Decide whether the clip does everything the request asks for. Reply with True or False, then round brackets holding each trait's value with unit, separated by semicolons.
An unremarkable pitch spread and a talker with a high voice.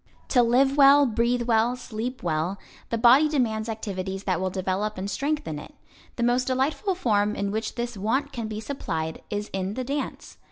True (4.4 semitones; 230 Hz)